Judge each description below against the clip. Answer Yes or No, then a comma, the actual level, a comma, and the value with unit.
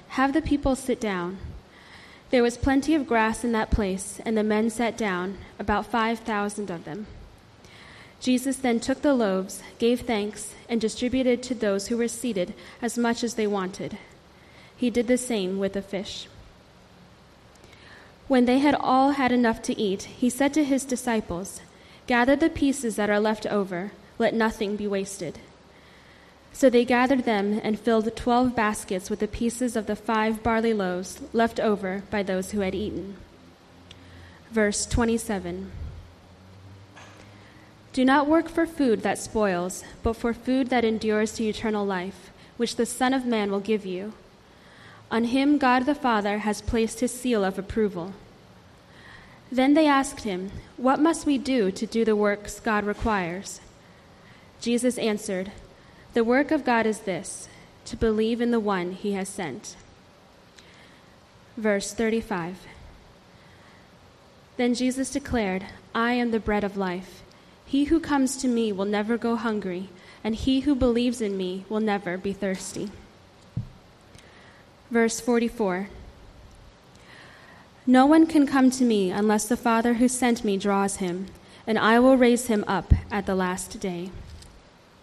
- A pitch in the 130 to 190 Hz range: No, high, 220 Hz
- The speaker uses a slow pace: No, average, 155 wpm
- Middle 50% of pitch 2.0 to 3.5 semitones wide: No, average, 3.9 semitones